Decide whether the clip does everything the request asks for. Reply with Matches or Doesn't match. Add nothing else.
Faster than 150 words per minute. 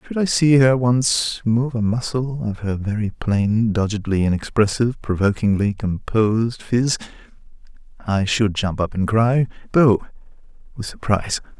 Doesn't match